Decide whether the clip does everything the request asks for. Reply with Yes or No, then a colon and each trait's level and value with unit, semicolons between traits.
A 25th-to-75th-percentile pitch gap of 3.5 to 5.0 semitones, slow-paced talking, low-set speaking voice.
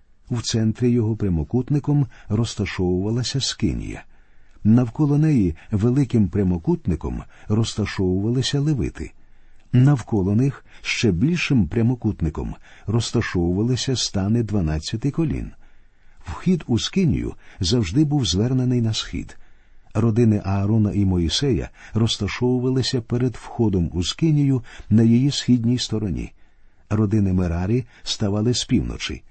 Yes: average, 3.9 semitones; slow, 95 wpm; low, 110 Hz